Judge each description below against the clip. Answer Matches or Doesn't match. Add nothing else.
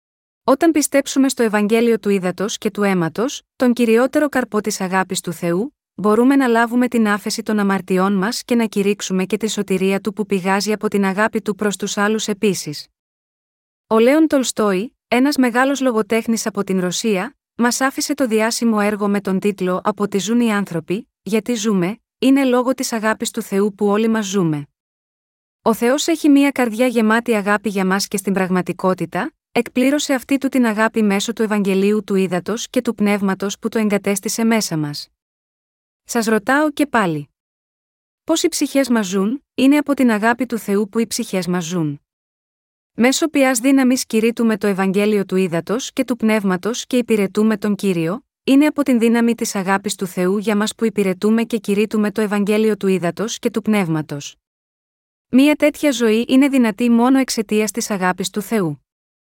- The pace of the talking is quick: Matches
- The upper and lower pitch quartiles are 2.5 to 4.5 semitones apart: Matches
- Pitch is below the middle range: Doesn't match